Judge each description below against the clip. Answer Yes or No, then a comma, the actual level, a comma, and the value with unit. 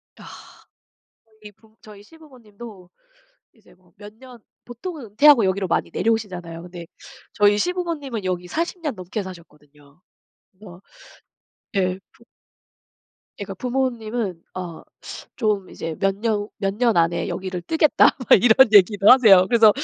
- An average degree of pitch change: Yes, average, 4.5 semitones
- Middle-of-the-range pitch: No, high, 205 Hz